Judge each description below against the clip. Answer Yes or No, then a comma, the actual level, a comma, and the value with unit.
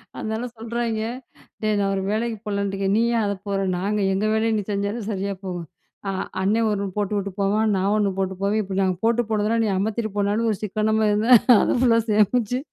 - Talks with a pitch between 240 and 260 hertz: No, high, 210 Hz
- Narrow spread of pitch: Yes, narrow, 1.9 semitones